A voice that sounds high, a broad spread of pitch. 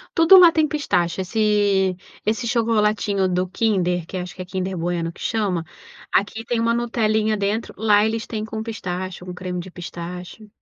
No: high, 205 Hz; average, 3.6 semitones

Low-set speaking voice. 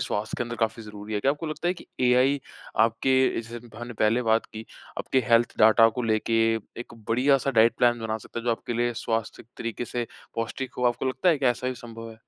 Yes: low, 120 Hz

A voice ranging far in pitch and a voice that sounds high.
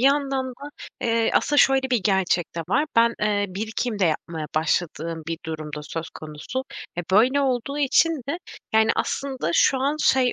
Yes: wide, 7.7 semitones; high, 230 Hz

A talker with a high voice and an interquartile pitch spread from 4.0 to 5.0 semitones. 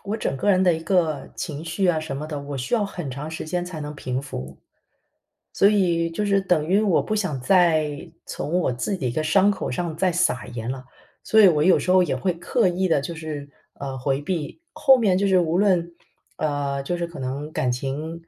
No: medium, 165 Hz; average, 4.6 semitones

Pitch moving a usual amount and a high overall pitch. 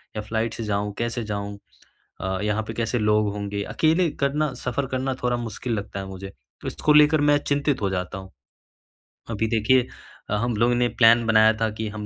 No: average, 3.5 semitones; low, 110 Hz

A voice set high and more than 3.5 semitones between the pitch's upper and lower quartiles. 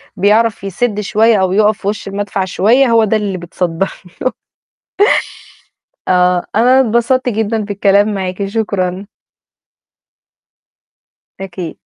No: high, 205 Hz; average, 2.8 semitones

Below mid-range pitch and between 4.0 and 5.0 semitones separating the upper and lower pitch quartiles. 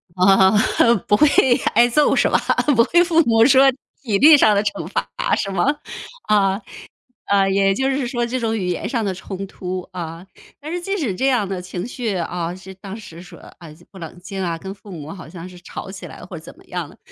No: high, 195 Hz; average, 4.6 semitones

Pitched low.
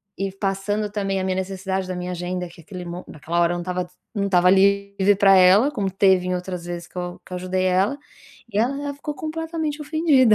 No: high, 190 Hz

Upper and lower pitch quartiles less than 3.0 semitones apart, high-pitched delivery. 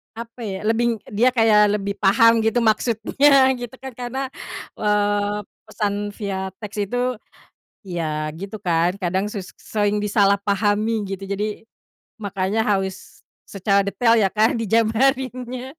Yes: narrow, 2.5 semitones; high, 210 Hz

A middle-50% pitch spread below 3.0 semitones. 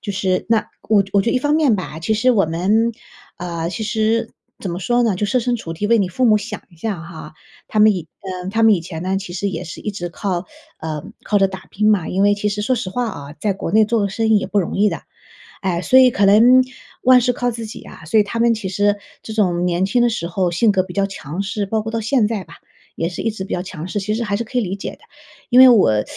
No: average, 3.6 semitones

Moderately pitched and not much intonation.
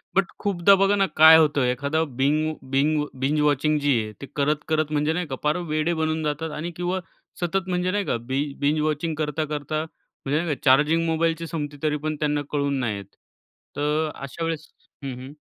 Yes: medium, 155 Hz; narrow, 1.9 semitones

